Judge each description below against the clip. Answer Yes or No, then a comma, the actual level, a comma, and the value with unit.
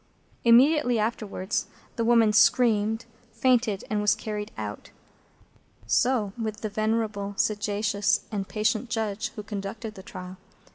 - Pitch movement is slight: Yes, narrow, 2.0 semitones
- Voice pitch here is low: No, high, 215 Hz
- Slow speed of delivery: Yes, slow, 125 wpm